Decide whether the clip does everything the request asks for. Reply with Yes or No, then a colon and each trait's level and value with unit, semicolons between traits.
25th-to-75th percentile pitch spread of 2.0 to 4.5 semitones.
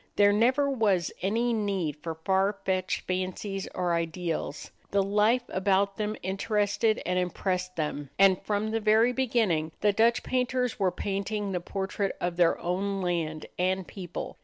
Yes: average, 2.9 semitones